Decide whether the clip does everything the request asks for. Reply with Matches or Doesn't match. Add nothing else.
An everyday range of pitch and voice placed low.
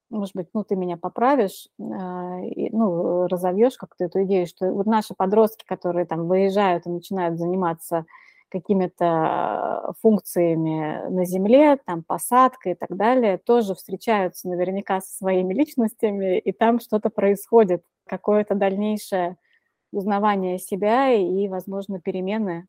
Doesn't match